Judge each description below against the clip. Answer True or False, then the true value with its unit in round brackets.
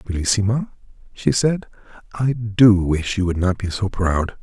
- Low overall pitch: True (105 Hz)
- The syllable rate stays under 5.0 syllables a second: True (4.4 syllables/s)